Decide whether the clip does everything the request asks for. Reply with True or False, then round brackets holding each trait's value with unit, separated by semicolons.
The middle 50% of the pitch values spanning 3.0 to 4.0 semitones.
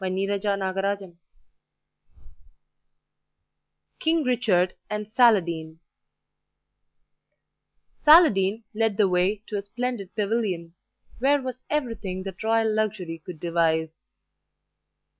True (3.7 semitones)